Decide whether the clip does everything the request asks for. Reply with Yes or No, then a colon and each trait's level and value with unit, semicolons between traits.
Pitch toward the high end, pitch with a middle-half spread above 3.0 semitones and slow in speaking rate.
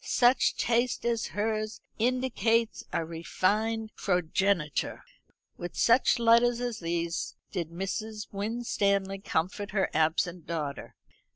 Yes: high, 205 Hz; average, 4.9 semitones; slow, 105 wpm